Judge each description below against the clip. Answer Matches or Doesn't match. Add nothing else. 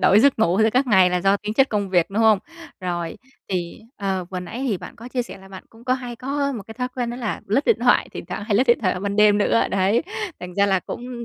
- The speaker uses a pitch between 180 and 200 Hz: Doesn't match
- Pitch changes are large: Doesn't match